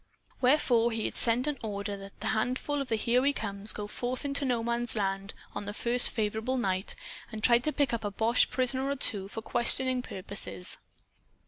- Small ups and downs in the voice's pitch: No, average, 3.7 semitones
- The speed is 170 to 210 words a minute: Yes, average, 200 wpm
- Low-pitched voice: No, high, 235 Hz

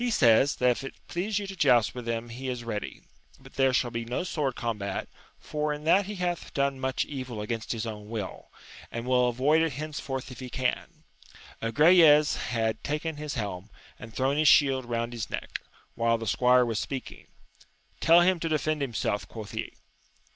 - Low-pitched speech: Yes, low, 130 Hz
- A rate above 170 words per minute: Yes, average, 190 wpm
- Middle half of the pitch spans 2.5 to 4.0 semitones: No, average, 4.5 semitones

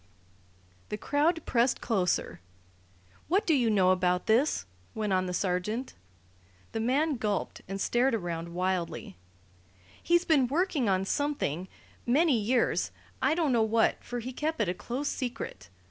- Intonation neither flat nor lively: No, wide, 7.2 semitones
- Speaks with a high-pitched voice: Yes, high, 230 Hz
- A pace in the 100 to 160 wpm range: Yes, average, 145 wpm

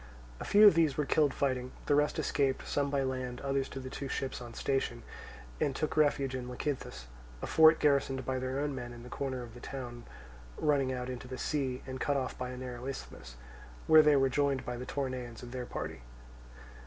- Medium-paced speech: No, fast, 215 wpm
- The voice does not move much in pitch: Yes, narrow, 2.0 semitones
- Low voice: Yes, low, 130 Hz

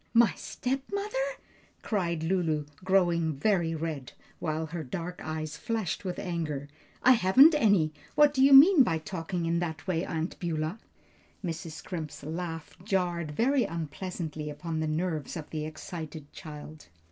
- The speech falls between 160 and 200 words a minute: No, average, 145 wpm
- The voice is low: No, medium, 170 Hz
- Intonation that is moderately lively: Yes, average, 3.6 semitones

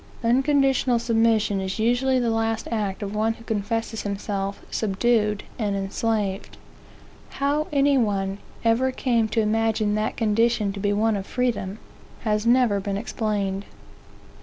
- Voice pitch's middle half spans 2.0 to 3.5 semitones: Yes, narrow, 2.6 semitones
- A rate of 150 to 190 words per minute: No, slow, 135 wpm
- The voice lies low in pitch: No, high, 220 Hz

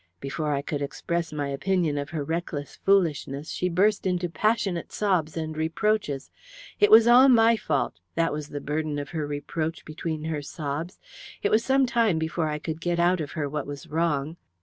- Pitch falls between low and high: Yes, medium, 160 Hz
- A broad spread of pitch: No, average, 3.7 semitones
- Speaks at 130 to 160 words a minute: No, average, 190 wpm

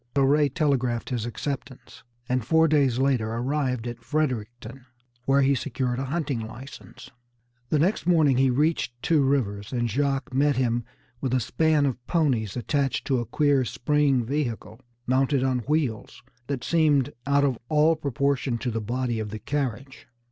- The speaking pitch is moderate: No, low, 130 Hz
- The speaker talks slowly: No, average, 160 wpm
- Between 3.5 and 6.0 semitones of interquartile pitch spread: No, average, 3.1 semitones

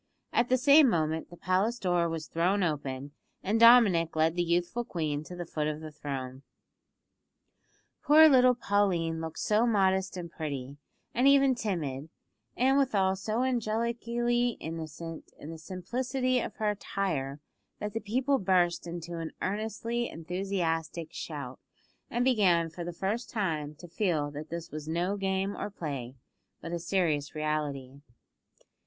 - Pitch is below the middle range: No, medium, 175 Hz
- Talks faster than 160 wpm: No, average, 150 wpm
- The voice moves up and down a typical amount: No, wide, 5.8 semitones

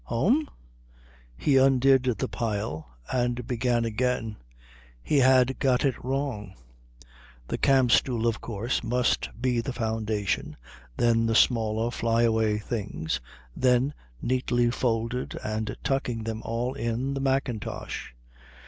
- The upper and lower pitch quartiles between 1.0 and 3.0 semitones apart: Yes, narrow, 2.5 semitones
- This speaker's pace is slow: Yes, slow, 120 wpm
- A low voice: Yes, low, 120 Hz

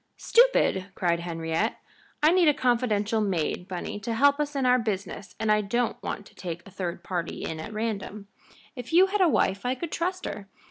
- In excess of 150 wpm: Yes, average, 200 wpm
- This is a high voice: Yes, high, 215 Hz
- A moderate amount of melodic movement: No, wide, 6.1 semitones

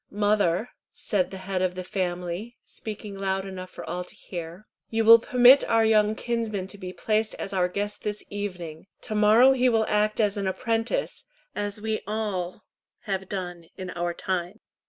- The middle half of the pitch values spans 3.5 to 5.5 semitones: No, average, 3.0 semitones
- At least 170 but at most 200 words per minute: Yes, average, 175 wpm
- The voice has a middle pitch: No, high, 205 Hz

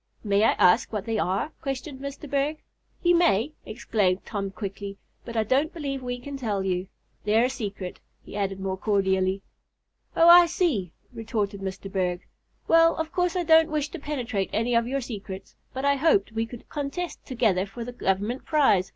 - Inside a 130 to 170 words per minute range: No, average, 185 wpm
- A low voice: No, high, 230 Hz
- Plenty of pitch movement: Yes, wide, 6.3 semitones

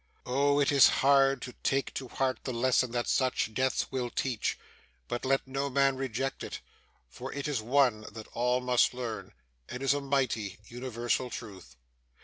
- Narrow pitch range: Yes, narrow, 2.3 semitones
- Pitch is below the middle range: Yes, low, 130 Hz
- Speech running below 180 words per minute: Yes, average, 170 wpm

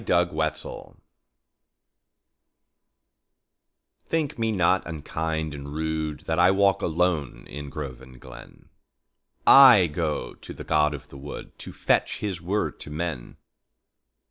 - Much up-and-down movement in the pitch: No, average, 3.6 semitones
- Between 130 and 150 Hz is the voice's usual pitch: No, very low, 80 Hz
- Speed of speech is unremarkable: No, slow, 115 wpm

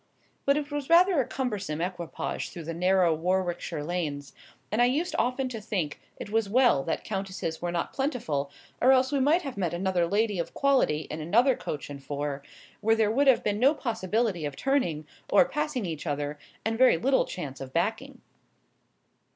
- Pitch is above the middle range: Yes, high, 200 Hz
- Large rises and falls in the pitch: Yes, wide, 7.8 semitones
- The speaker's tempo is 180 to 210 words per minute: Yes, average, 185 wpm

